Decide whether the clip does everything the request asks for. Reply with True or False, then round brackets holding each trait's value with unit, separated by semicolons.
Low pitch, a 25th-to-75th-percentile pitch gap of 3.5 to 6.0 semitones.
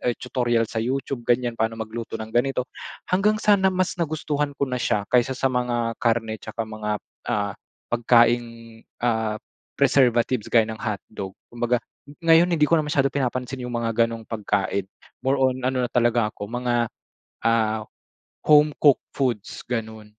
False (120 Hz; 2.9 semitones)